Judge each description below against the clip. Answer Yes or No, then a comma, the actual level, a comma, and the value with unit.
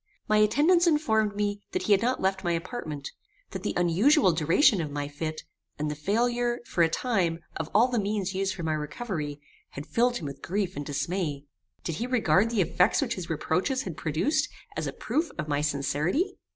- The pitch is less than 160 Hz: No, high, 190 Hz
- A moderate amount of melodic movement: No, wide, 7.4 semitones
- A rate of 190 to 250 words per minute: Yes, average, 200 wpm